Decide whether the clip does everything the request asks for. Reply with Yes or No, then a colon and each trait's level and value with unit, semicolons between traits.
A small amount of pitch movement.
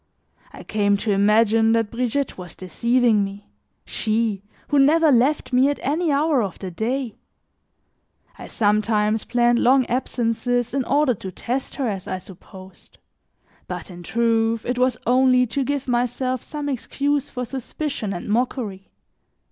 No: average, 3.8 semitones